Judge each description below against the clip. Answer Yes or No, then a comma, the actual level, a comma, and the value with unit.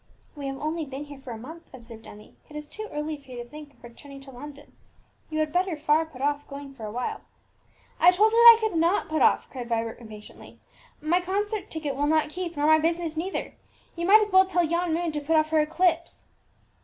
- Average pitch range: Yes, average, 3.8 semitones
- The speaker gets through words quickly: Yes, fast, 235 wpm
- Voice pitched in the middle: No, very high, 310 Hz